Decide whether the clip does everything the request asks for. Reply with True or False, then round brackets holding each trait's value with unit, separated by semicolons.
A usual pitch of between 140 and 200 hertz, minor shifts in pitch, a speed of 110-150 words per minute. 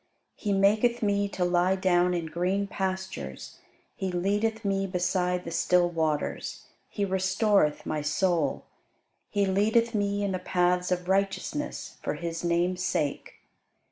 True (185 Hz; 2.3 semitones; 140 wpm)